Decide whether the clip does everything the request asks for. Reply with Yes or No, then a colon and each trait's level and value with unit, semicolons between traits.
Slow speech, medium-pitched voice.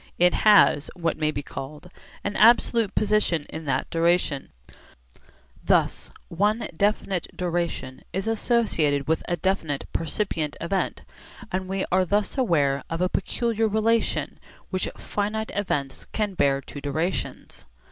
Yes: slow, 130 wpm; medium, 180 Hz